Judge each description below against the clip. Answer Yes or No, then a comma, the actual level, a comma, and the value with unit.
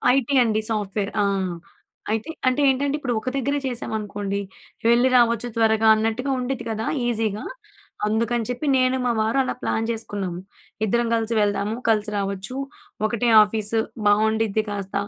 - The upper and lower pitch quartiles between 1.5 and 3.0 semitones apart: Yes, narrow, 2.5 semitones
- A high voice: Yes, high, 225 Hz